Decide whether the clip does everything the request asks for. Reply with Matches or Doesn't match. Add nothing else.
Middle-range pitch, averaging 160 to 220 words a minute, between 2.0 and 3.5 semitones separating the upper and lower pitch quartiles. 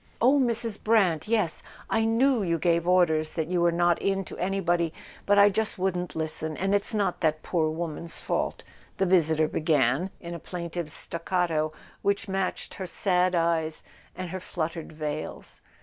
Matches